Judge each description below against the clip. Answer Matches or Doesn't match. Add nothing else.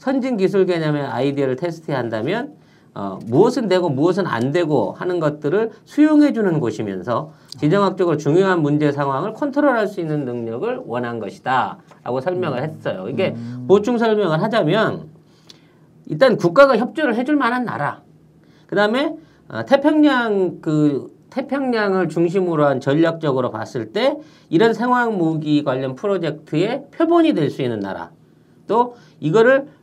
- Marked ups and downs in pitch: Matches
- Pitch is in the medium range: Matches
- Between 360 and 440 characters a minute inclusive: Doesn't match